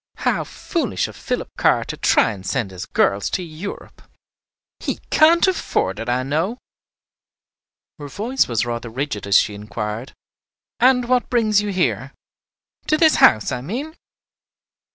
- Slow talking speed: No, average, 150 wpm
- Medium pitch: Yes, medium, 150 Hz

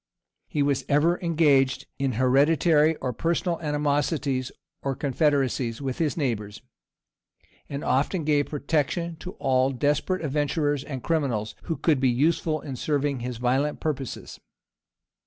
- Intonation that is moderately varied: Yes, average, 3.0 semitones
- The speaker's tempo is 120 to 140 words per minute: Yes, slow, 135 wpm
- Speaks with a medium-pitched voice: Yes, medium, 145 Hz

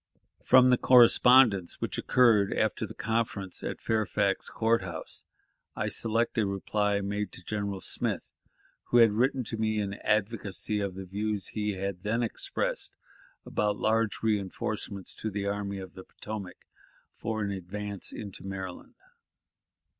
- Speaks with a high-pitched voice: No, low, 105 Hz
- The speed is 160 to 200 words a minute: No, average, 145 wpm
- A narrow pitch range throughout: Yes, narrow, 2.2 semitones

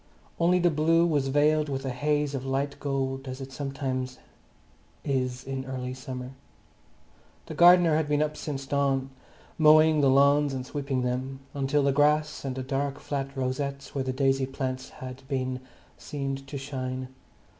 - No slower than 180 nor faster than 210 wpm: No, average, 165 wpm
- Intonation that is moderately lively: No, narrow, 1.8 semitones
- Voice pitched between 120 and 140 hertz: Yes, low, 135 Hz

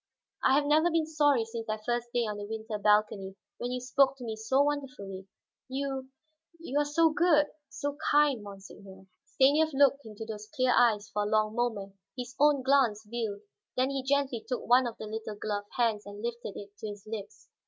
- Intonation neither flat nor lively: Yes, average, 4.7 semitones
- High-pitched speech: Yes, high, 240 Hz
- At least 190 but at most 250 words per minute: Yes, average, 195 wpm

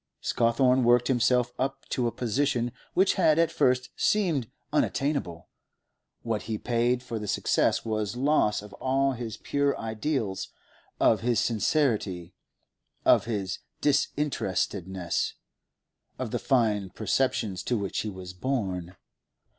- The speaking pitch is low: Yes, low, 120 Hz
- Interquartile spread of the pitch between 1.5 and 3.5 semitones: No, average, 4.4 semitones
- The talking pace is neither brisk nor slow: No, slow, 125 wpm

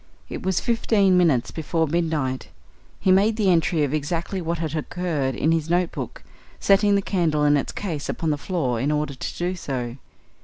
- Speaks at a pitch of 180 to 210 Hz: No, medium, 165 Hz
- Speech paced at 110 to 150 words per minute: No, average, 185 wpm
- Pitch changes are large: No, average, 3.8 semitones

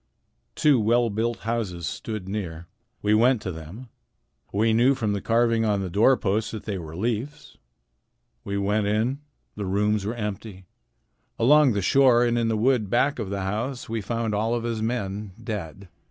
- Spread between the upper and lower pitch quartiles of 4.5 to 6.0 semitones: No, average, 2.9 semitones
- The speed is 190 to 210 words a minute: No, average, 180 wpm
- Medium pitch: No, low, 110 Hz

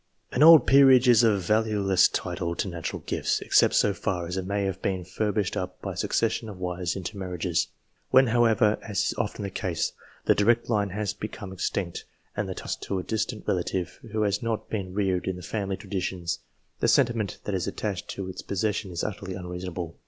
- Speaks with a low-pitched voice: Yes, very low, 95 Hz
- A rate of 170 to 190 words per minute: No, fast, 205 wpm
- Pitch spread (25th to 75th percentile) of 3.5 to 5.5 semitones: No, average, 2.9 semitones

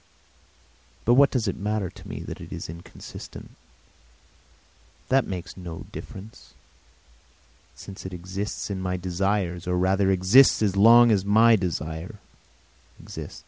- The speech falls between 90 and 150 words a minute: Yes, slow, 135 wpm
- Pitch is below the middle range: Yes, very low, 95 Hz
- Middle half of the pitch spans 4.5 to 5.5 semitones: No, average, 3.0 semitones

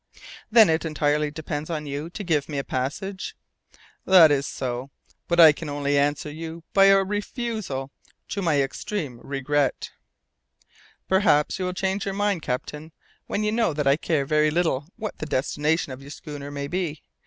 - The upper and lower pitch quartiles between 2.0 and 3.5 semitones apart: No, average, 4.7 semitones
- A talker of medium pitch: Yes, medium, 155 Hz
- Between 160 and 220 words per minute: Yes, average, 175 wpm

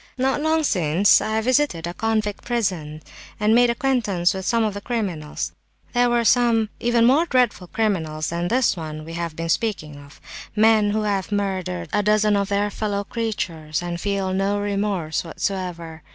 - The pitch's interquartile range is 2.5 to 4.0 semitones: No, average, 4.7 semitones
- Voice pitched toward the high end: Yes, high, 205 Hz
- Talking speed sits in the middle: Yes, average, 165 wpm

